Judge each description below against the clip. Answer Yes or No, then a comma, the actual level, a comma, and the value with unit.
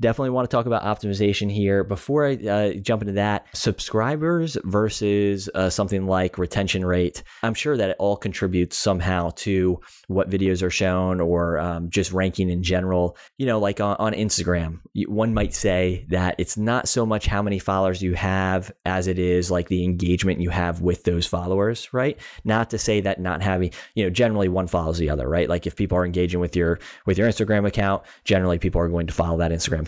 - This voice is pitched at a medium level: No, very low, 95 Hz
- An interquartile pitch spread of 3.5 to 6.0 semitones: No, narrow, 2.6 semitones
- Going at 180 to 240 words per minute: Yes, fast, 205 wpm